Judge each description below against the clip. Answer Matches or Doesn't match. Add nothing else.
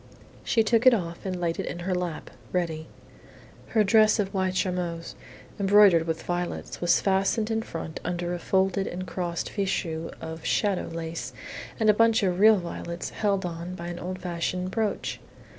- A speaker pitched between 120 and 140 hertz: Doesn't match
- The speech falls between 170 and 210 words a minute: Matches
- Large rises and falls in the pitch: Doesn't match